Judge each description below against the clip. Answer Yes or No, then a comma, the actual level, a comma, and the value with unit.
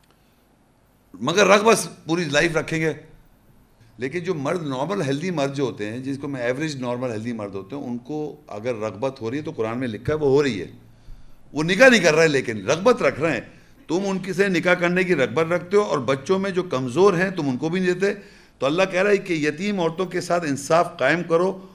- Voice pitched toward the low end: No, medium, 160 Hz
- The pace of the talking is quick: Yes, fast, 235 wpm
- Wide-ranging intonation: Yes, wide, 6.2 semitones